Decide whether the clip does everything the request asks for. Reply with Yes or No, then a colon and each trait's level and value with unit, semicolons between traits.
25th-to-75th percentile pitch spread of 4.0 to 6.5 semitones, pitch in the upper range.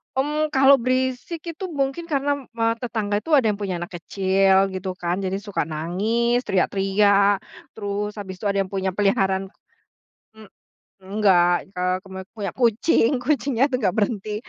Yes: average, 4.3 semitones; high, 205 Hz